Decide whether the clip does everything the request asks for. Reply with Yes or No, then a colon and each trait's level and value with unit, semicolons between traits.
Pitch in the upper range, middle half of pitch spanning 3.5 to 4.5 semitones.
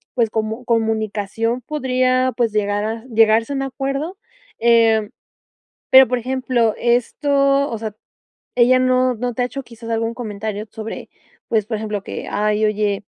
No: high, 230 Hz; average, 2.8 semitones